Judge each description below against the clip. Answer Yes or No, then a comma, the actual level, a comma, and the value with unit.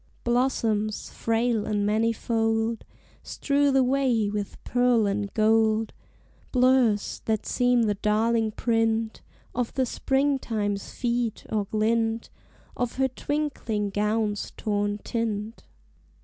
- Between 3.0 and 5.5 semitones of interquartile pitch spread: No, narrow, 2.5 semitones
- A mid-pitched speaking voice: No, high, 225 Hz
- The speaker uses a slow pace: Yes, slow, 105 wpm